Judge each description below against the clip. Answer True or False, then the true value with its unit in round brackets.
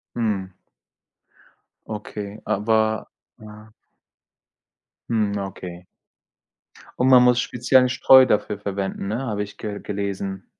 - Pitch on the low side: True (105 Hz)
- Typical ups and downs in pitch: False (2.2 semitones)